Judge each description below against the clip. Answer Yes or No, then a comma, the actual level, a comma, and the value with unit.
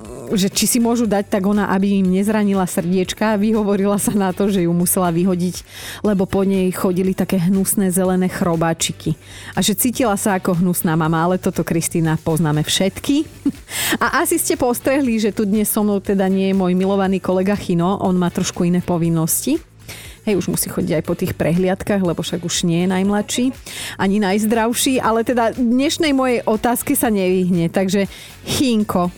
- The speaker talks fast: Yes, fast, 175 wpm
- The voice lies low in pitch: No, high, 195 Hz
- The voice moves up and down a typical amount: Yes, average, 3.1 semitones